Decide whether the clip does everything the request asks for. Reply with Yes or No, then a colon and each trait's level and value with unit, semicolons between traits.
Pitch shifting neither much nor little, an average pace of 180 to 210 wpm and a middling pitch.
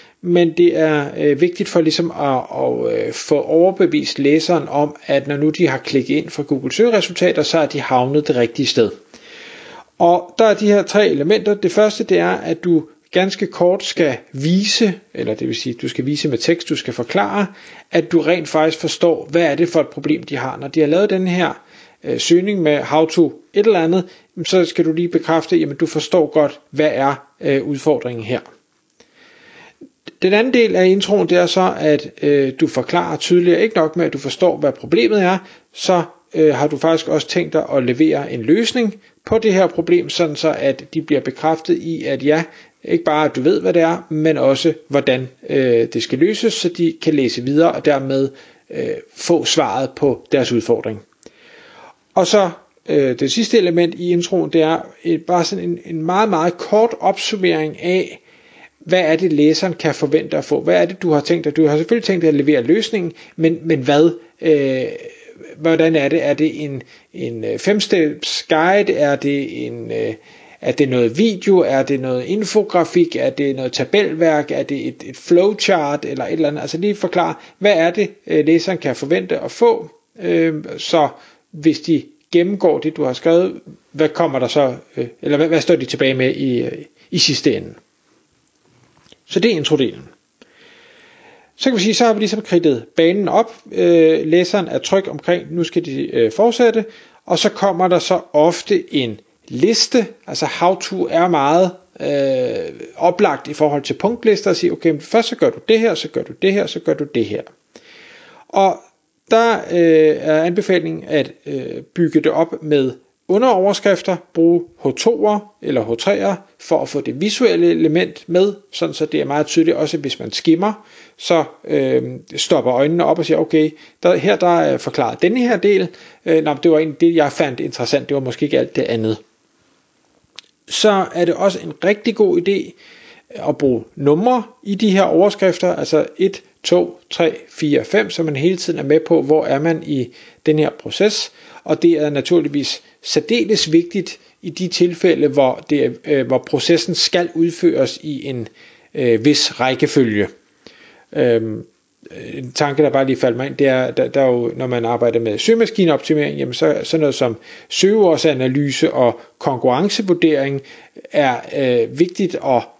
Yes: average, 4.3 semitones; average, 190 wpm; medium, 165 Hz